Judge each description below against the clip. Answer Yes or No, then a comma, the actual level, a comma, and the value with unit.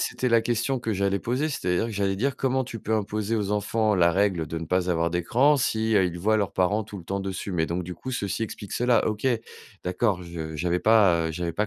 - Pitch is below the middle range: Yes, low, 100 Hz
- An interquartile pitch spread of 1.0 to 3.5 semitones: No, average, 4.1 semitones